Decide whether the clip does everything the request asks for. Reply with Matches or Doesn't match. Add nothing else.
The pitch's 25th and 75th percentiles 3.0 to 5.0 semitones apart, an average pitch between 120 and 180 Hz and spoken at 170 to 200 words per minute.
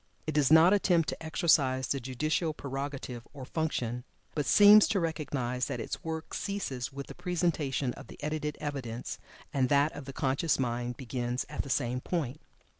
Matches